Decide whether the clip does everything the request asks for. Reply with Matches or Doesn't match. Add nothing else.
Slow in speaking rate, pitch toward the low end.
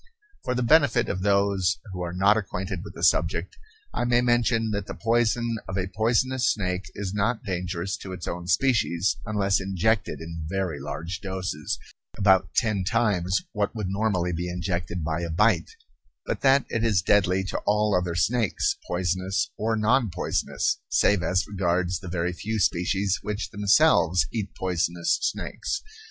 Doesn't match